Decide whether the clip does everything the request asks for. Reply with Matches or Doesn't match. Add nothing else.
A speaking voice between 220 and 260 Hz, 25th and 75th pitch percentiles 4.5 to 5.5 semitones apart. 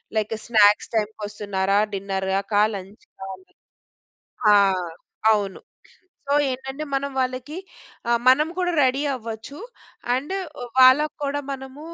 Matches